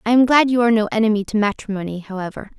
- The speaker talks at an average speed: No, fast, 230 wpm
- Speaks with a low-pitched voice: No, high, 220 Hz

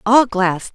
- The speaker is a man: No, female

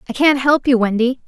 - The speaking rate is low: No, fast, 235 wpm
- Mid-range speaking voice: No, very high, 255 Hz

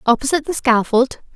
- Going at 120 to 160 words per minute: Yes, slow, 135 wpm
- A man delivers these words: No, female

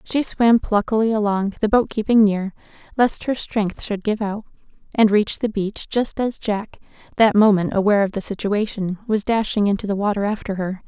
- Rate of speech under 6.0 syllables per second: Yes, 5.2 syllables/s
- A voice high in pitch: Yes, high, 210 Hz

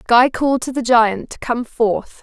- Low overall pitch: No, high, 240 Hz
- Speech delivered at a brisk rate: Yes, fast, 215 wpm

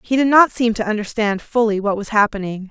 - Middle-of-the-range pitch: No, high, 220 Hz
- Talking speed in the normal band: No, fast, 220 wpm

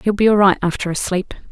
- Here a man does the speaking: No, female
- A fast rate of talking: Yes, fast, 280 wpm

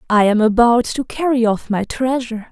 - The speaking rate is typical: Yes, average, 190 wpm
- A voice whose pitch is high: Yes, high, 235 Hz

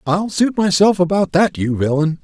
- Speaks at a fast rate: No, average, 190 wpm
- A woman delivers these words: No, male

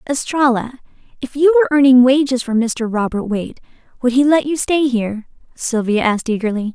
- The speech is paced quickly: No, average, 170 wpm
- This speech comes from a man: No, female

